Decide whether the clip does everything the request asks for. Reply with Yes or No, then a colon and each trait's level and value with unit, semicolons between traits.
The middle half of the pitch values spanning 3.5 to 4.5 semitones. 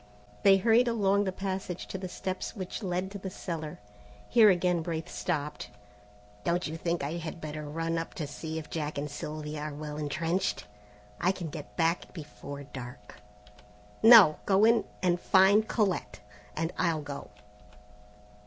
Yes: average, 3.9 semitones